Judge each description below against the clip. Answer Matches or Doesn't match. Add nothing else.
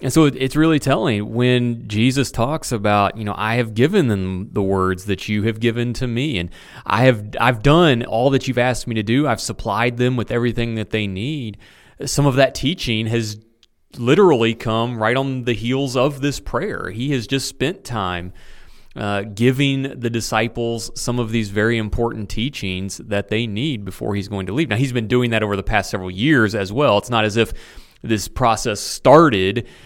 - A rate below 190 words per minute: Doesn't match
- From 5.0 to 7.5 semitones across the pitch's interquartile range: Doesn't match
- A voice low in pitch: Matches